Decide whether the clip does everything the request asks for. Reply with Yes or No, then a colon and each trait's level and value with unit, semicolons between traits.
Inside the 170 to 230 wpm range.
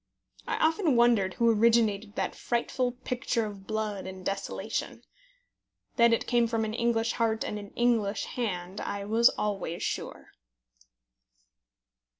No: slow, 135 wpm